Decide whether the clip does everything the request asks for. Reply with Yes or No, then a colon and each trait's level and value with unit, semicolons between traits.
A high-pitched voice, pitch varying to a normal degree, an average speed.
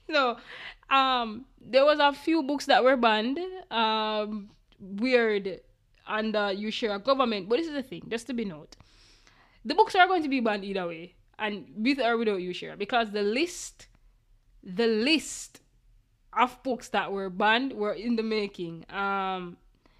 Yes: high, 220 Hz; average, 4.8 semitones; average, 175 wpm